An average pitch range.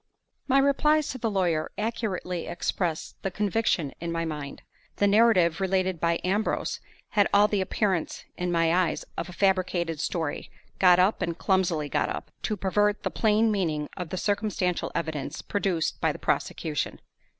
Yes: average, 3.6 semitones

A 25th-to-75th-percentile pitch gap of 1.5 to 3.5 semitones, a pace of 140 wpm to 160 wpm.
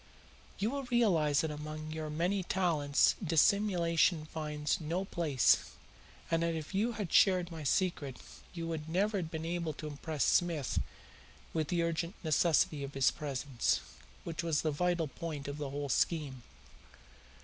Yes: average, 2.8 semitones; average, 155 wpm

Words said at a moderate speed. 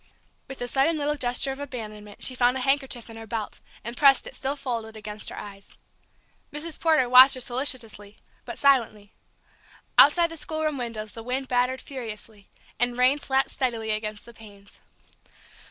Yes: average, 170 wpm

